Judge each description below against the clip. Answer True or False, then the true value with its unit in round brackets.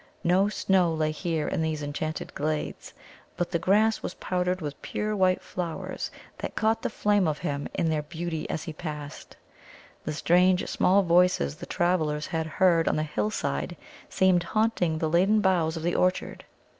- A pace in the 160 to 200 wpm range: True (170 wpm)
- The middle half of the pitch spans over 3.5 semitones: False (3.1 semitones)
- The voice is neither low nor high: True (170 Hz)